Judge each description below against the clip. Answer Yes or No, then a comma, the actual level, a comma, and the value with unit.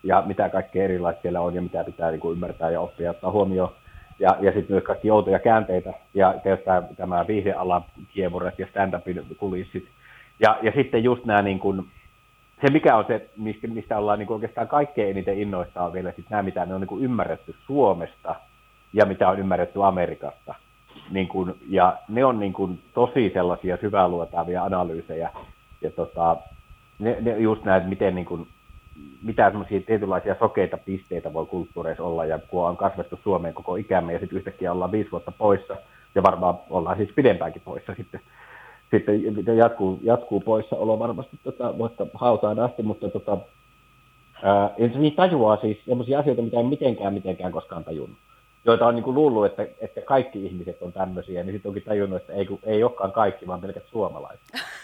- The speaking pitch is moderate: No, low, 100 Hz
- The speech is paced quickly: Yes, fast, 175 wpm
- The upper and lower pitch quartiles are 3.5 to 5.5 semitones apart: Yes, average, 3.9 semitones